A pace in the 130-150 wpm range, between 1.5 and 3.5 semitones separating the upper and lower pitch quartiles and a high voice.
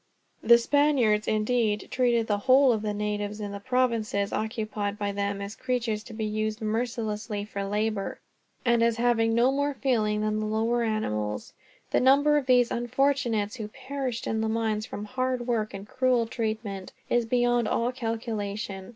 No: average, 170 wpm; average, 2.7 semitones; high, 225 Hz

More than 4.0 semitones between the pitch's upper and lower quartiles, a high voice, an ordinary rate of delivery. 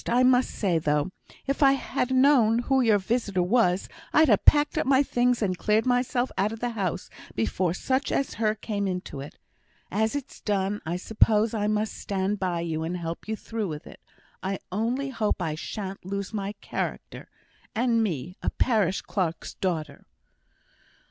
Yes: average, 4.9 semitones; high, 210 Hz; average, 175 wpm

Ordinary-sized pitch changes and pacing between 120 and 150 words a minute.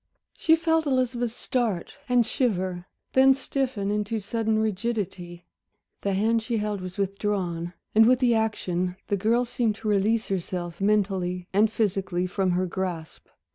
Yes: average, 3.9 semitones; average, 145 wpm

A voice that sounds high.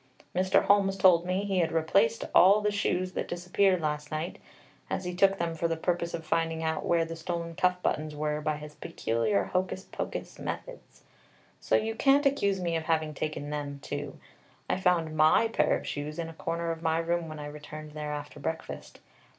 No: medium, 165 Hz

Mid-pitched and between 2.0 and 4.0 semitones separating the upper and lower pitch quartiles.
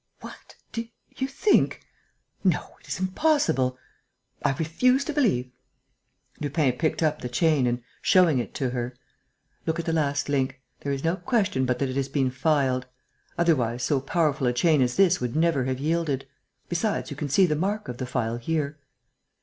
No: medium, 145 Hz; average, 4.7 semitones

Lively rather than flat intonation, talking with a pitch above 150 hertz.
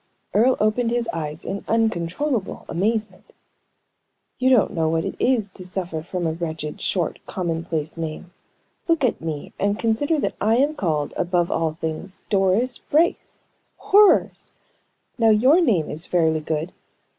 Yes: wide, 6.1 semitones; medium, 185 Hz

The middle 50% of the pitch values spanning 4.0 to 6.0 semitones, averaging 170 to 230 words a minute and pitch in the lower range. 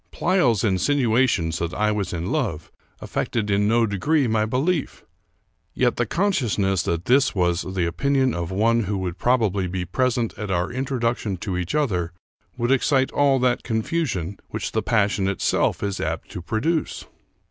No: wide, 5.5 semitones; average, 160 wpm; low, 110 Hz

